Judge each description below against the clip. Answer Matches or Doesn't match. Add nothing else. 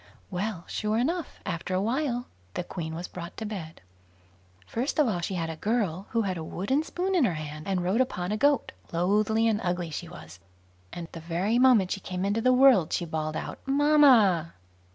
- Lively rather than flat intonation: Matches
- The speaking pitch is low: Doesn't match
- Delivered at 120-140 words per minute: Doesn't match